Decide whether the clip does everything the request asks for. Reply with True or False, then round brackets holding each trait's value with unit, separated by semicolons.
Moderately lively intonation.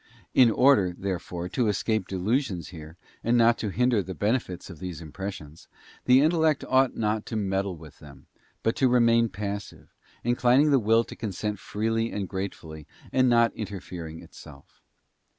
True (4.5 semitones)